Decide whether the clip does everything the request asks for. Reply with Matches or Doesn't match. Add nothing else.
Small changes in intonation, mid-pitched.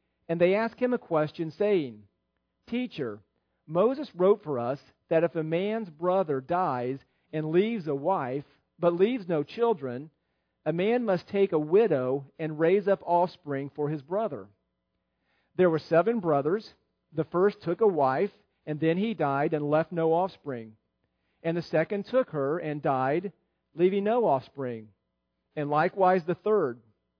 Doesn't match